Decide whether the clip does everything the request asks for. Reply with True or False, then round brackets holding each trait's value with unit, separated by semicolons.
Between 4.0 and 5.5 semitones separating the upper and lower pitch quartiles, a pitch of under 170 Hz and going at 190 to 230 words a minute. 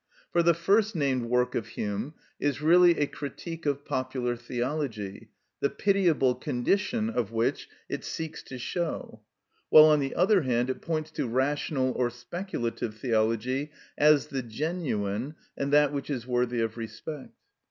False (4.5 semitones; 135 Hz; 155 wpm)